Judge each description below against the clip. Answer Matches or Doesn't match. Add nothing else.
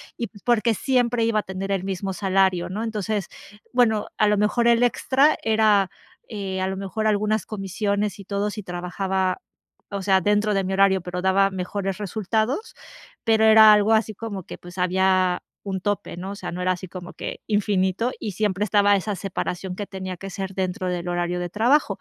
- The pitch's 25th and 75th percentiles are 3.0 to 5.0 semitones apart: Doesn't match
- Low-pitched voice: Doesn't match